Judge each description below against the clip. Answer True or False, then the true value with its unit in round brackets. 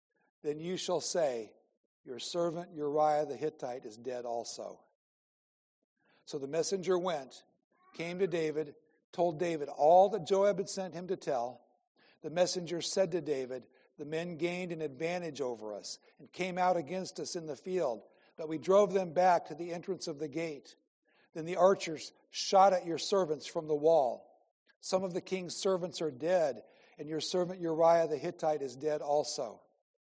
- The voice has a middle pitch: True (170 Hz)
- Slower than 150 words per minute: False (170 wpm)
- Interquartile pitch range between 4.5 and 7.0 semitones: False (2.9 semitones)